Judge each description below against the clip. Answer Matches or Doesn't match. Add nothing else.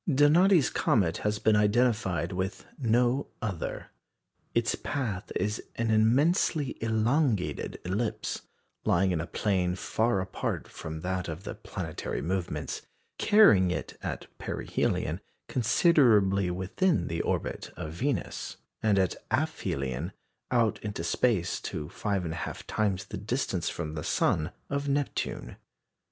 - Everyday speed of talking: Doesn't match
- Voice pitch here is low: Matches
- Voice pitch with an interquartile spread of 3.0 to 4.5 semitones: Doesn't match